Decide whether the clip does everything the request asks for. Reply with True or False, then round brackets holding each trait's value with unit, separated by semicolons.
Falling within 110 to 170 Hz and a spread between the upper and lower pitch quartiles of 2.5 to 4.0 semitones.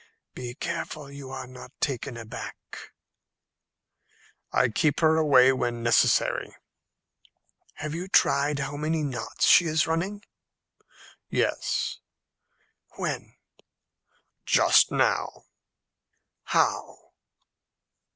True (140 Hz; 3.6 semitones)